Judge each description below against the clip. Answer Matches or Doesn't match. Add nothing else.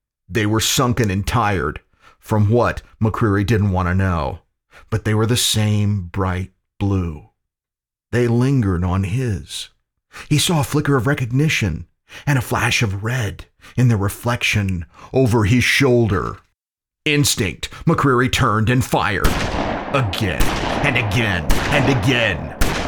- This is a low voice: Matches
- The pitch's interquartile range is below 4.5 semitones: Doesn't match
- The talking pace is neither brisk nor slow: Doesn't match